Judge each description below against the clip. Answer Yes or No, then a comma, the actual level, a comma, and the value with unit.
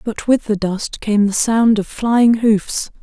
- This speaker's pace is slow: No, average, 200 wpm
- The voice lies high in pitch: Yes, high, 215 Hz